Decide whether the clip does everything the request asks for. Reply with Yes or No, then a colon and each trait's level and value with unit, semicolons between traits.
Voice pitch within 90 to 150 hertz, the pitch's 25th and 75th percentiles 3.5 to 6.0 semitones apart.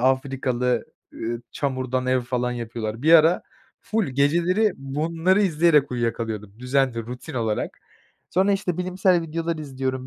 Yes: low, 135 Hz; average, 5.2 semitones